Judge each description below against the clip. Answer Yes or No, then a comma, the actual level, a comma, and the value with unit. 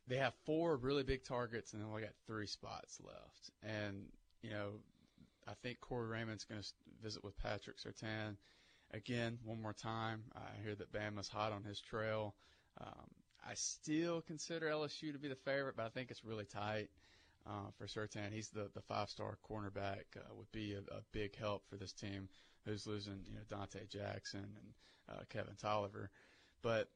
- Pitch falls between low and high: No, low, 105 Hz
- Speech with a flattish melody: Yes, narrow, 2.1 semitones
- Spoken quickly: No, average, 185 wpm